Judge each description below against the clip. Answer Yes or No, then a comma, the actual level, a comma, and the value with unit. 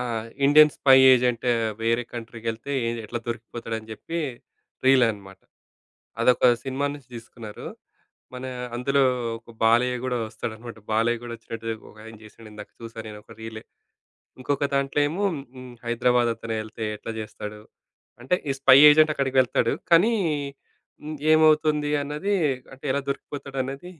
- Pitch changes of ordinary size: Yes, average, 3.5 semitones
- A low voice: Yes, low, 120 Hz